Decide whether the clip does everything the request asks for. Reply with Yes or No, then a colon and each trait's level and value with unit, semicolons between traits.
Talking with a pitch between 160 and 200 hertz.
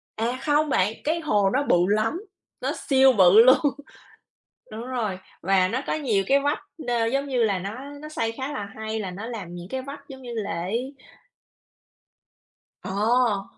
No: high, 230 Hz